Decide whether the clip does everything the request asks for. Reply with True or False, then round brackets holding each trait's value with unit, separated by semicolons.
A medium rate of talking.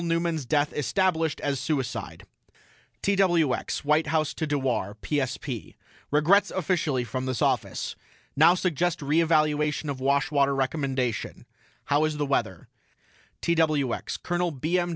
False (125 wpm)